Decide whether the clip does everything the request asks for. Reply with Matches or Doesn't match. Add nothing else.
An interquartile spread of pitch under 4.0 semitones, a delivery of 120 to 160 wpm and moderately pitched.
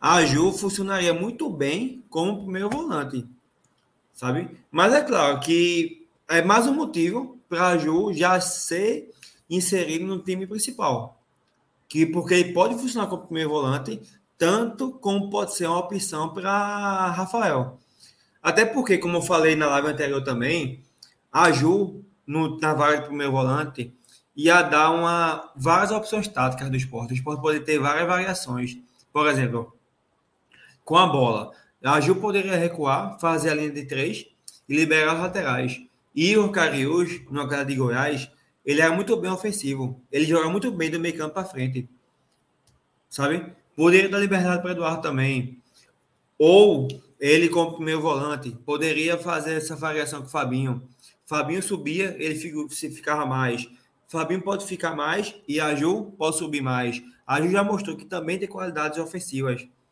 Doesn't match